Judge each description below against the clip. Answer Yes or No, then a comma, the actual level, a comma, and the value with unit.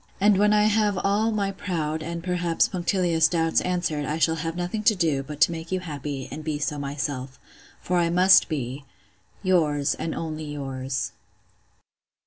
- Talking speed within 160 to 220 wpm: Yes, average, 170 wpm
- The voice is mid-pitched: Yes, medium, 165 Hz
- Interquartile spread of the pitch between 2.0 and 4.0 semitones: Yes, average, 3.7 semitones